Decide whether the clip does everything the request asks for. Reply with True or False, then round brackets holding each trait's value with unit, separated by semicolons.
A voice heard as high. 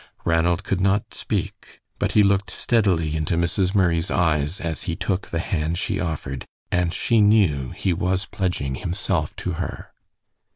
False (90 Hz)